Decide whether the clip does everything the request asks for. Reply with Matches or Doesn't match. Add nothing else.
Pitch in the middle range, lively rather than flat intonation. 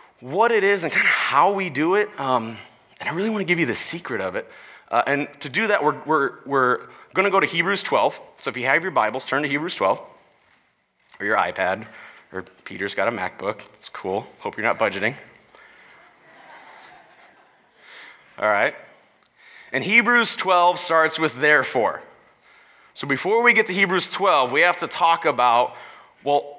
Matches